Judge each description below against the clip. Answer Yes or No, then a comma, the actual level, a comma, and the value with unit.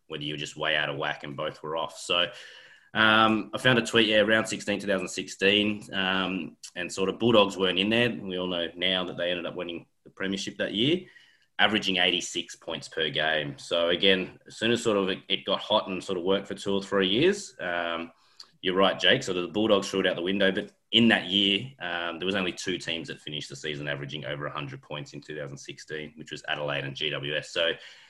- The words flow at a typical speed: No, fast, 230 wpm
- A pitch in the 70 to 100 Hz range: Yes, very low, 95 Hz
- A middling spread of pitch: Yes, average, 3.4 semitones